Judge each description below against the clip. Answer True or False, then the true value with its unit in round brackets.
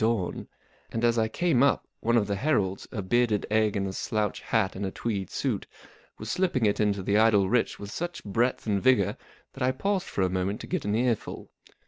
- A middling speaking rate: False (215 wpm)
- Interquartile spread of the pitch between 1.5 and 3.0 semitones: False (3.4 semitones)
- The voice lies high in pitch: False (110 Hz)